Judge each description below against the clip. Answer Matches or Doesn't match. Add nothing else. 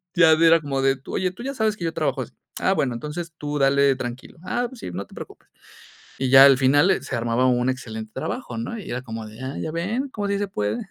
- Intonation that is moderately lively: Doesn't match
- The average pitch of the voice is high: Doesn't match